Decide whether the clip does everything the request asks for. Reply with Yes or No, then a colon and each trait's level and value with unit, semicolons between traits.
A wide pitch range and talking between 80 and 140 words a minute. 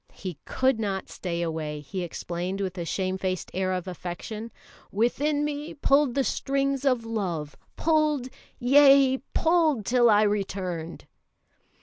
Yes: wide, 7.1 semitones; slow, 135 wpm